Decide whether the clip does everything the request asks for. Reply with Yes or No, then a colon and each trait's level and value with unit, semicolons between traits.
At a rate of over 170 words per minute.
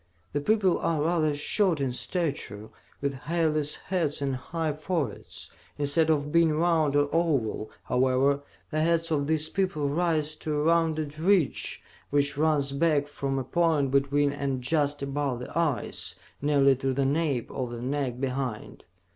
No: average, 155 wpm